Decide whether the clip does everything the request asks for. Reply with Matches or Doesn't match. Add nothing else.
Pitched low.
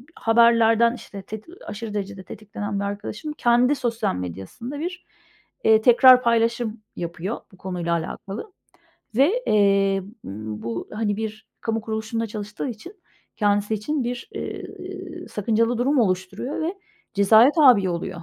Doesn't match